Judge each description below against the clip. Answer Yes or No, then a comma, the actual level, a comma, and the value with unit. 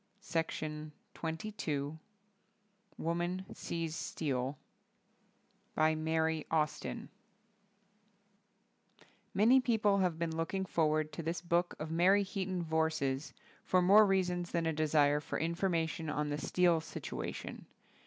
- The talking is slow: Yes, slow, 115 wpm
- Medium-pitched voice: Yes, medium, 165 Hz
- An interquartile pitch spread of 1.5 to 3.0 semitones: Yes, narrow, 2.6 semitones